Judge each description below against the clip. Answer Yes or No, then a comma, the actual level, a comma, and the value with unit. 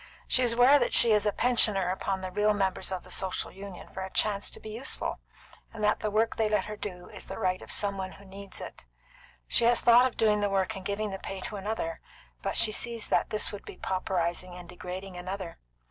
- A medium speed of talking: No, fast, 240 wpm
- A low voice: No, high, 200 Hz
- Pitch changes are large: No, narrow, 2.4 semitones